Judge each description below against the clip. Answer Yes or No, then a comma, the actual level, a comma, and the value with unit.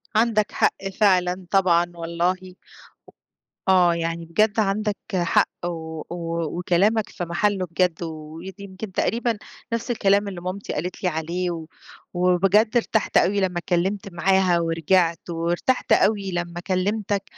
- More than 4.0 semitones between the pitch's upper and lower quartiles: No, average, 2.7 semitones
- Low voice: No, medium, 185 Hz